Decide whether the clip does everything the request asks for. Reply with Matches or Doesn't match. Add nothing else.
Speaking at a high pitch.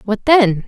Matches